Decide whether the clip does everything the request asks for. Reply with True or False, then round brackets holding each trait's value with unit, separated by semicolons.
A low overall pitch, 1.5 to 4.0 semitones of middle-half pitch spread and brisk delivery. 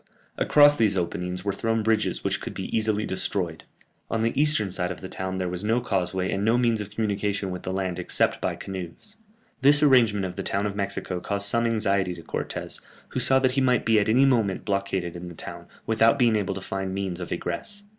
True (100 Hz; 3.3 semitones; 220 wpm)